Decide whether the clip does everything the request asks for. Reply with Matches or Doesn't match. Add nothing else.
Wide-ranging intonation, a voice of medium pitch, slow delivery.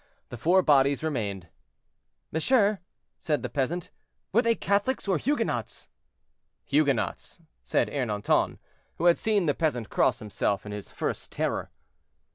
Matches